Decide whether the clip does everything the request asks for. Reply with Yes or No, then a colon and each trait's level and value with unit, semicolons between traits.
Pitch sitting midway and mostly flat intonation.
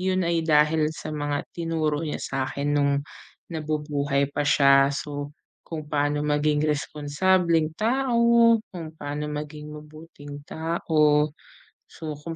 Yes: medium, 150 Hz; narrow, 1.9 semitones